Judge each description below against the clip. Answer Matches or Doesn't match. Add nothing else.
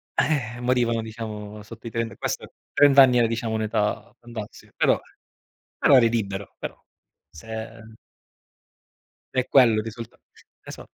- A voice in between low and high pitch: Doesn't match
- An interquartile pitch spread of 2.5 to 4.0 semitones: Doesn't match